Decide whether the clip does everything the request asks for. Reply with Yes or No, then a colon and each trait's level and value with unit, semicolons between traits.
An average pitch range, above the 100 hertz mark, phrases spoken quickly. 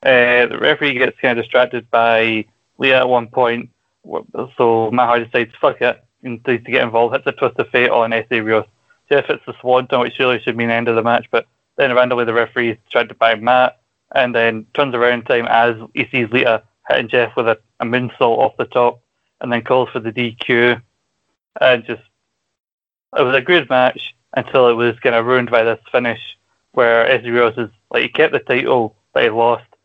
No: narrow, 1.4 semitones; low, 120 Hz; fast, 215 wpm